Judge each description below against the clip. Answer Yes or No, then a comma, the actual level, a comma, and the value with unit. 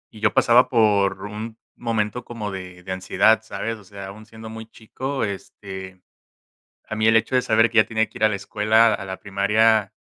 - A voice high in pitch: No, low, 110 Hz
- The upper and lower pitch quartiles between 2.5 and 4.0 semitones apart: No, narrow, 2.1 semitones